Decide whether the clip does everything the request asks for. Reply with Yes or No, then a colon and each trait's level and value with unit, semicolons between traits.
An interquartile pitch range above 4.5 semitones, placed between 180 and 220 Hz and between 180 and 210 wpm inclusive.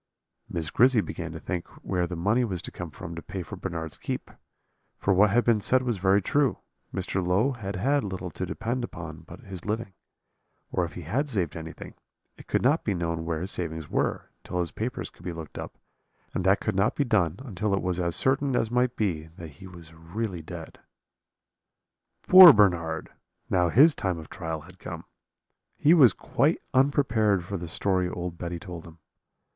No: average, 5.1 semitones; very low, 95 Hz; average, 195 wpm